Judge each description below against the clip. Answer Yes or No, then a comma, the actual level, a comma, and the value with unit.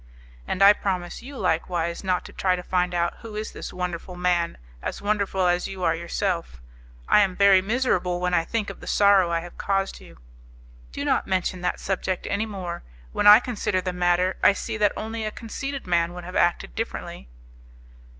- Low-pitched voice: No, medium, 185 Hz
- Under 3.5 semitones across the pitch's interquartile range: Yes, narrow, 2.5 semitones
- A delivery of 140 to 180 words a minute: No, average, 195 wpm